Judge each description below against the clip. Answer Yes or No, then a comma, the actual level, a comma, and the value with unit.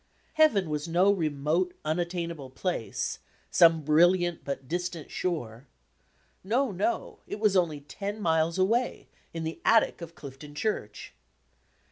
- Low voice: No, medium, 170 Hz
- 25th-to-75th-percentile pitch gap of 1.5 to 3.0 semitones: No, average, 3.7 semitones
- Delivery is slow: Yes, slow, 130 wpm